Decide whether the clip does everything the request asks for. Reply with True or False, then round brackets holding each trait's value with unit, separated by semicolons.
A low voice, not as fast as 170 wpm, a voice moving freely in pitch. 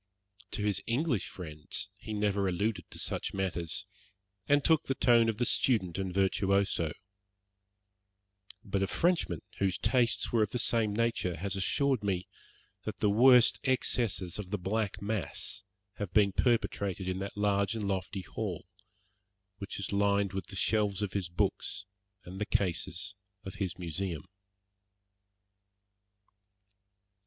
False (100 Hz; 140 wpm; 2.7 semitones)